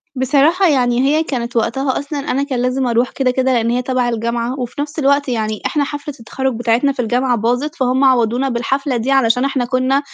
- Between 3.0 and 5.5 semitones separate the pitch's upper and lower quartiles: No, narrow, 2.5 semitones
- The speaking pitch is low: No, very high, 255 Hz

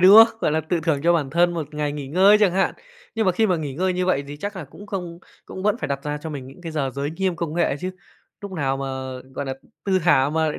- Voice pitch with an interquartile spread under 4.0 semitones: No, average, 4.5 semitones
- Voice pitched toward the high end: No, medium, 165 Hz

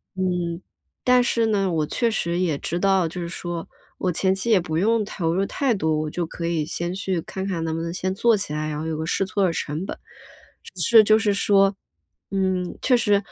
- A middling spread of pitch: Yes, average, 3.2 semitones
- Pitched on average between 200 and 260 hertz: No, medium, 185 Hz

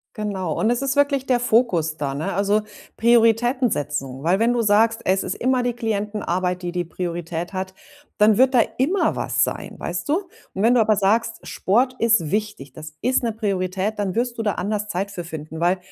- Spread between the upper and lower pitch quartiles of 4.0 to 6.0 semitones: Yes, average, 4.7 semitones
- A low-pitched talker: No, high, 210 Hz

